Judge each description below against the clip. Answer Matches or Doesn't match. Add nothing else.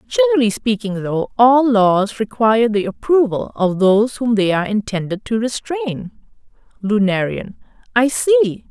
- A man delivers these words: Doesn't match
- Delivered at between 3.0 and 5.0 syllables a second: Matches